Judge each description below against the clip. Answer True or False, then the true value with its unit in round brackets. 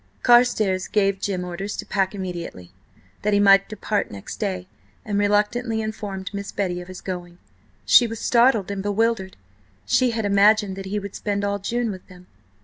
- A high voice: True (200 Hz)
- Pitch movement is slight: True (2.2 semitones)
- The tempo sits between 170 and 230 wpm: True (175 wpm)